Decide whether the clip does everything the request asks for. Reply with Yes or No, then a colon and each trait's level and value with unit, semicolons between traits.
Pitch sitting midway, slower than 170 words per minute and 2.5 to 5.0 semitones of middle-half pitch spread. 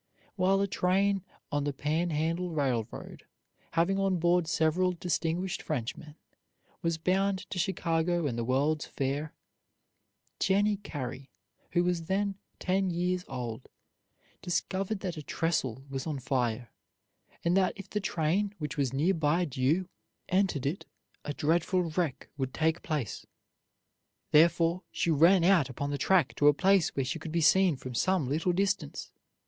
Yes: medium, 165 Hz; average, 150 wpm; average, 4.3 semitones